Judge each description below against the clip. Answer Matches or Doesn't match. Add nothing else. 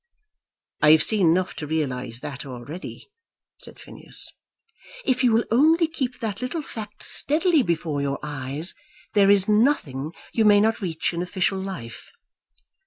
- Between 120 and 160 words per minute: Matches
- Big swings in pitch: Matches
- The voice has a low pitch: Doesn't match